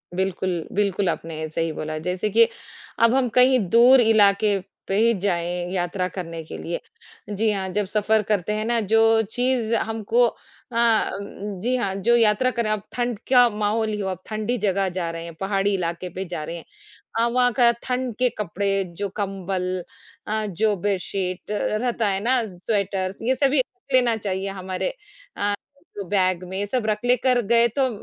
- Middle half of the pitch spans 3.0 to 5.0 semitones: Yes, average, 3.7 semitones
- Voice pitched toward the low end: No, high, 210 Hz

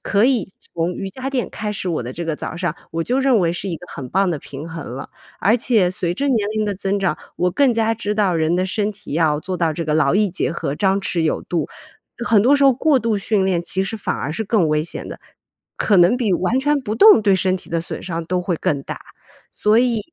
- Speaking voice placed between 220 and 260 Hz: No, high, 190 Hz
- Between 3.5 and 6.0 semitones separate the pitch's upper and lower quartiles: Yes, average, 4.7 semitones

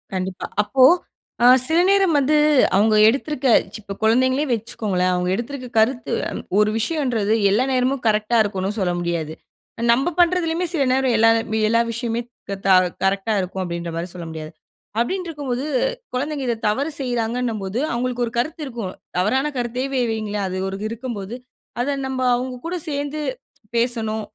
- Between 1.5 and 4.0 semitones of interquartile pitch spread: No, average, 4.6 semitones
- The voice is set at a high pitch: Yes, high, 235 Hz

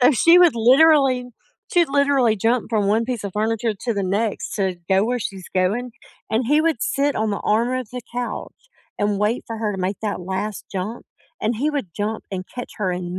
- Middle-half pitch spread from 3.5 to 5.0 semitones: Yes, average, 3.8 semitones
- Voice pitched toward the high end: Yes, high, 225 Hz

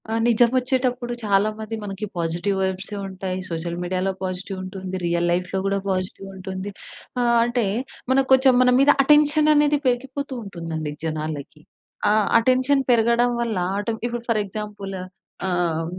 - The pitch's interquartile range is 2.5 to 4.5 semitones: No, average, 5.0 semitones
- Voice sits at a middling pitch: No, high, 205 Hz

